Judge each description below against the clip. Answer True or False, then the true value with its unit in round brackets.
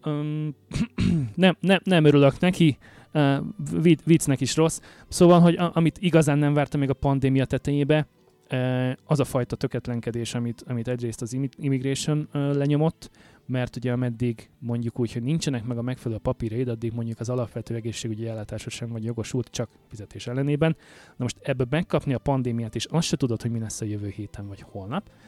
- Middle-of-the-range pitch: False (130 Hz)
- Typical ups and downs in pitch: True (4.2 semitones)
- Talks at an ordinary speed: False (175 wpm)